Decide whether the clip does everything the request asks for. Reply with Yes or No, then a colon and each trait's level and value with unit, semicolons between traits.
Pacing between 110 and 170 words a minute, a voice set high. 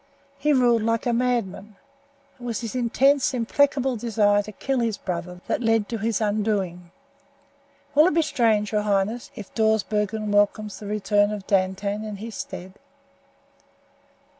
Yes: average, 150 wpm; high, 215 Hz